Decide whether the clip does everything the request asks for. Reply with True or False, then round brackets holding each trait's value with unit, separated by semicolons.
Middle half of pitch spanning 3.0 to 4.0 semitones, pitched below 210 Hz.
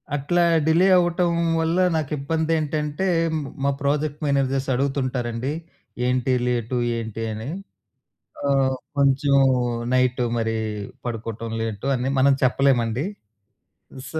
True (3.4 semitones; 135 Hz)